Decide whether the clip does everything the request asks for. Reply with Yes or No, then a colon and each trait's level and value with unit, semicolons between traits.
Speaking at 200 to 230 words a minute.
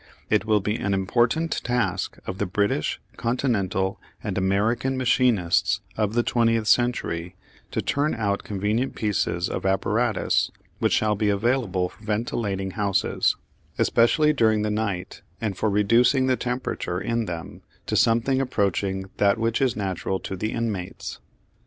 No: average, 145 wpm